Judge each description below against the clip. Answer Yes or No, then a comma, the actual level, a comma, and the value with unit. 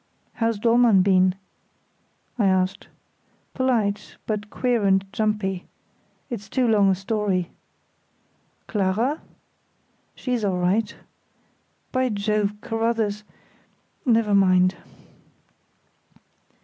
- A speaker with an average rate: No, slow, 85 wpm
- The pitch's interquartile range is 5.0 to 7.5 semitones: No, average, 2.9 semitones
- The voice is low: No, high, 210 Hz